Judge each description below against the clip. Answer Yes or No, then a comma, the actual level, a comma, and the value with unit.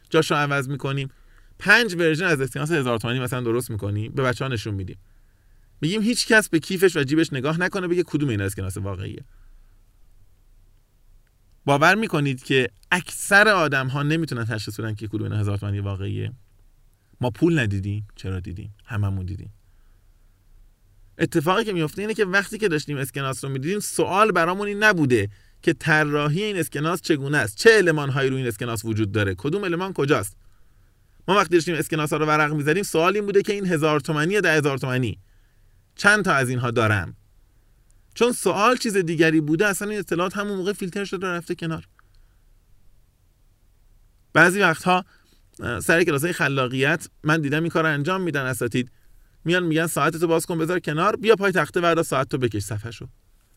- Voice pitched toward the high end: No, low, 135 Hz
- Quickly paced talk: Yes, fast, 165 wpm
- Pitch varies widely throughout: Yes, wide, 8.5 semitones